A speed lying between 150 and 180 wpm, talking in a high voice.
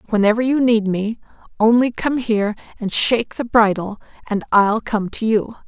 Yes: average, 170 wpm; high, 220 Hz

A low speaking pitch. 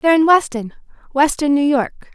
No: very high, 285 Hz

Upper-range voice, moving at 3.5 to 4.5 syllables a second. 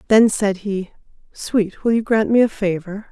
Yes: high, 205 Hz; 4.4 syllables/s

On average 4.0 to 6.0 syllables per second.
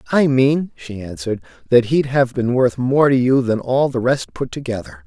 Yes: 4.9 syllables/s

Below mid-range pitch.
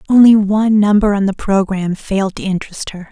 No: high, 200 Hz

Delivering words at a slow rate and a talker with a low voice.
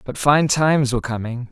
No: average, 200 wpm; low, 130 Hz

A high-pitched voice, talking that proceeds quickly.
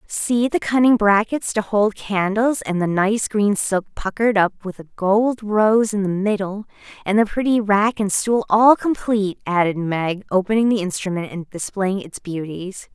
No: high, 205 Hz; average, 175 wpm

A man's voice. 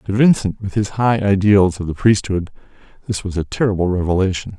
Yes: male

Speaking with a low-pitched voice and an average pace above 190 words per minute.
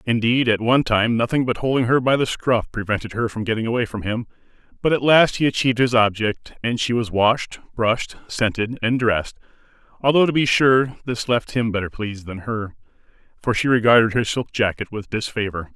Yes: low, 115 Hz; average, 200 wpm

